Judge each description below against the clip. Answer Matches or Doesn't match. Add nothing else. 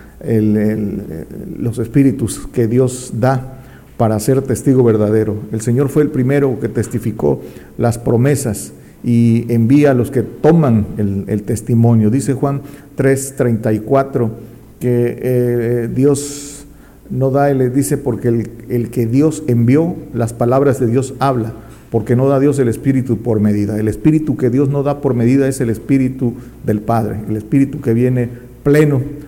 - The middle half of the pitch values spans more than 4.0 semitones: Doesn't match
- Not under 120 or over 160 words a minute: Matches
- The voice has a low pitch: Matches